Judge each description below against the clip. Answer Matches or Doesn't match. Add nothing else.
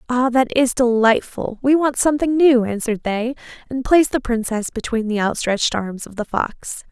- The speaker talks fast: Doesn't match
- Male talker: Doesn't match